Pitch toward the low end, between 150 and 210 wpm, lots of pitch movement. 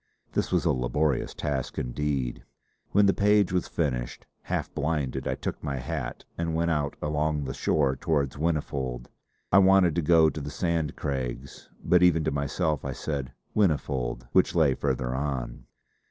No: very low, 75 Hz; average, 165 wpm; average, 3.8 semitones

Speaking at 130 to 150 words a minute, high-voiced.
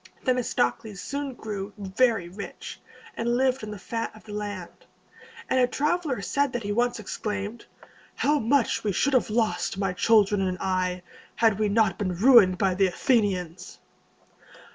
No: average, 160 wpm; high, 210 Hz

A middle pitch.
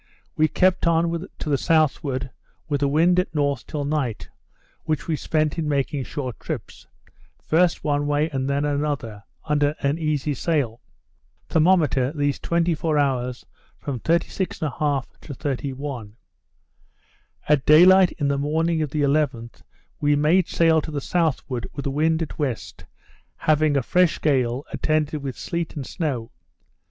Yes: medium, 150 Hz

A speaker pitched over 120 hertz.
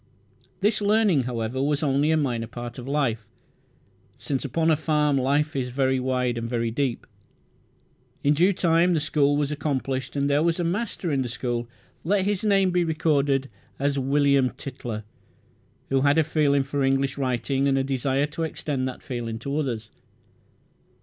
Yes: medium, 140 Hz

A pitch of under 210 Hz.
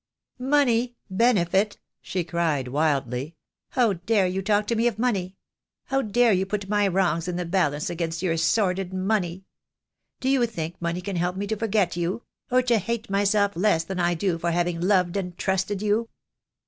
Yes: high, 190 Hz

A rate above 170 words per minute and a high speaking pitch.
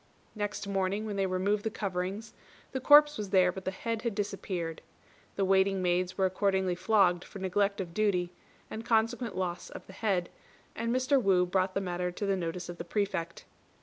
Yes: average, 190 wpm; high, 195 Hz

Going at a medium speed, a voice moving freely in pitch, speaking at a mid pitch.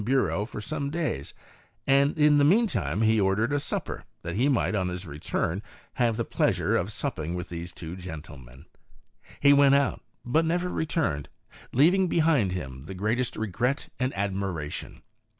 No: average, 170 wpm; wide, 8.3 semitones; low, 110 Hz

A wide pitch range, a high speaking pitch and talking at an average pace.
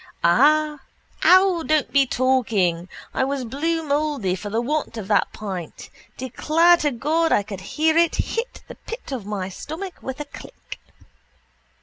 Yes: wide, 6.8 semitones; very high, 280 Hz; average, 155 wpm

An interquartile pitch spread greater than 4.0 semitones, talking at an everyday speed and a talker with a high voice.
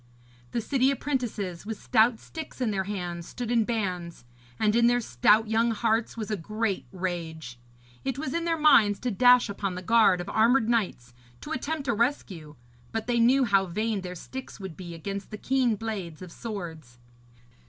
Yes: average, 4.7 semitones; average, 185 wpm; high, 215 Hz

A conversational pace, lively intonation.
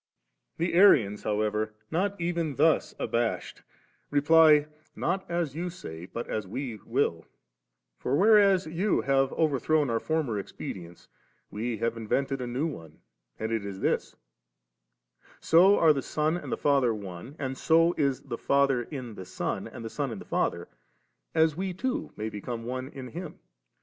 Yes: average, 175 wpm; wide, 6.9 semitones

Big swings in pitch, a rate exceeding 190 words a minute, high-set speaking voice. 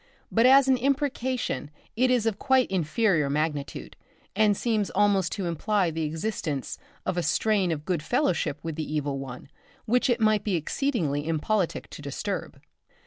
No: wide, 6.9 semitones; average, 160 wpm; high, 195 Hz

